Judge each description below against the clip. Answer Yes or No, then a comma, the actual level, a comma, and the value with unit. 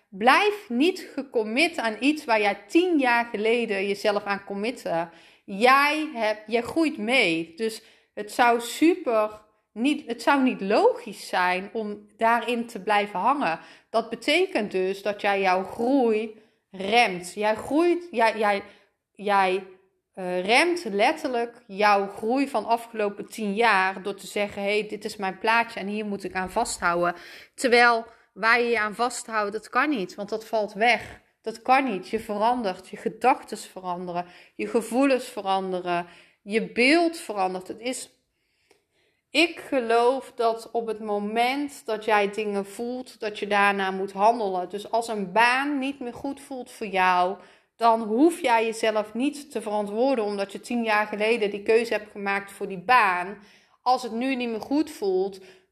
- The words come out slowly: No, average, 165 wpm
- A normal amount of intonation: Yes, average, 3.3 semitones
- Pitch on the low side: No, high, 220 Hz